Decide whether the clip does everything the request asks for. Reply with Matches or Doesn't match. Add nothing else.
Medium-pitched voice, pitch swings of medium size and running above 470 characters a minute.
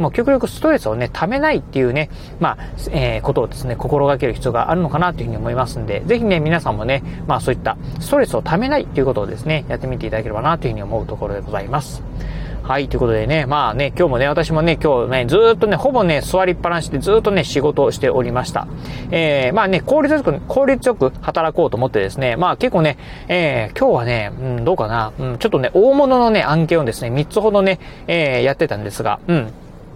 Doesn't match